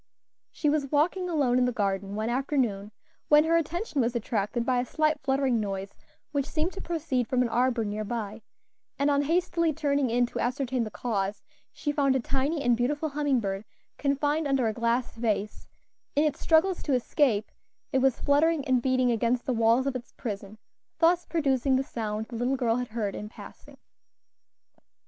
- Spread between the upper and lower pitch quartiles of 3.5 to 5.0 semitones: Yes, average, 4.1 semitones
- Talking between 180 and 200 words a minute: Yes, average, 185 wpm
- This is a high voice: Yes, very high, 255 Hz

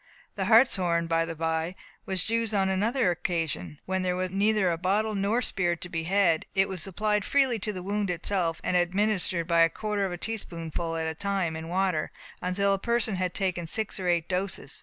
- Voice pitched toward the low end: No, medium, 185 Hz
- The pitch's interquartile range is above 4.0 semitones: No, average, 3.2 semitones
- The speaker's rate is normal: No, fast, 210 wpm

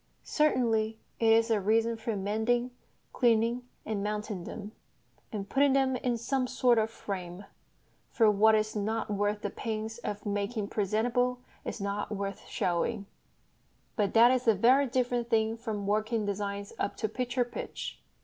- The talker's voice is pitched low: No, high, 220 Hz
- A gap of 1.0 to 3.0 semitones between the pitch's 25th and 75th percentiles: Yes, average, 2.7 semitones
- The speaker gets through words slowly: No, average, 155 wpm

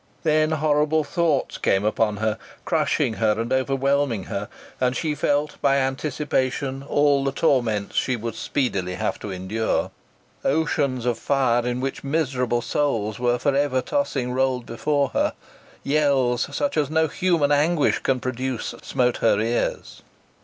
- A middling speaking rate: Yes, average, 145 wpm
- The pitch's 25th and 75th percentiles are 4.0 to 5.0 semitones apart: No, average, 3.5 semitones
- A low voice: Yes, low, 130 Hz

